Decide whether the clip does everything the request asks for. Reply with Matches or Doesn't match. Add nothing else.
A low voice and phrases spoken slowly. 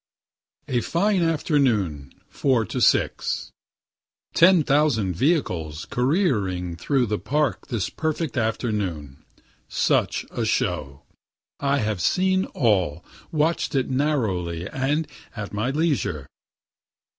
Matches